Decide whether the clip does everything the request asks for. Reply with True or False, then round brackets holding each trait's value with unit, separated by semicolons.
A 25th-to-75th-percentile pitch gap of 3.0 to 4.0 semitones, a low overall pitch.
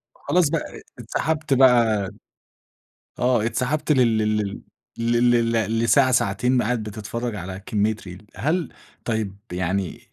True (3.6 semitones; 115 Hz)